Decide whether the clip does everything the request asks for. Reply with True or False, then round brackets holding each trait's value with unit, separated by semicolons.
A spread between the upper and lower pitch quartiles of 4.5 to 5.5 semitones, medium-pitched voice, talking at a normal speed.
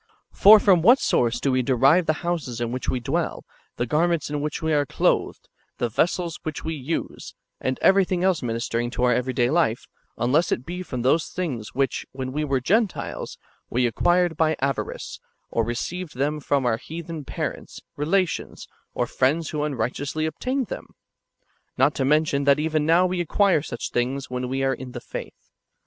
True (4.8 semitones; 145 Hz; 190 wpm)